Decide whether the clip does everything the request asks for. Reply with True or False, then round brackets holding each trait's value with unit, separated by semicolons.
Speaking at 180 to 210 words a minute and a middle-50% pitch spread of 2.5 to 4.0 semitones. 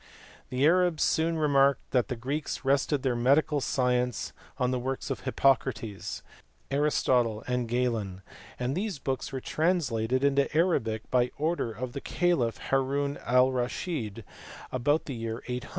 False (145 wpm; 2.9 semitones)